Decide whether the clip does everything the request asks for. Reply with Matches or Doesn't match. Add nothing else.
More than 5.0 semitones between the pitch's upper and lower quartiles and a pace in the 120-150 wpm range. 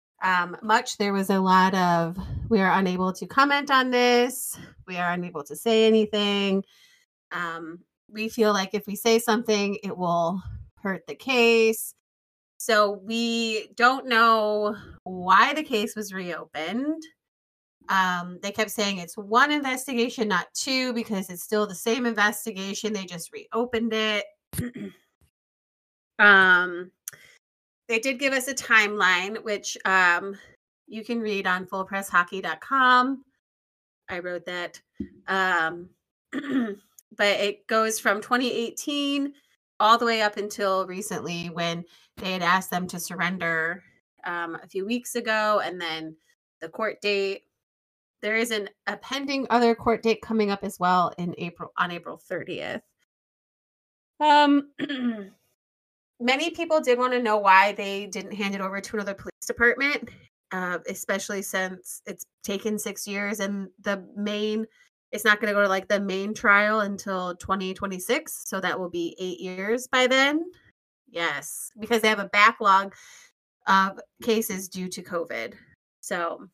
Doesn't match